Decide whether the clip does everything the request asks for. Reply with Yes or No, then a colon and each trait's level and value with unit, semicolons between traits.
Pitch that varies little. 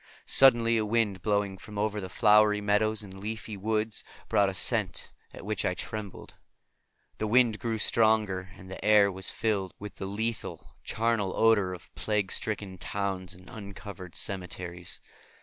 Yes: narrow, 2.3 semitones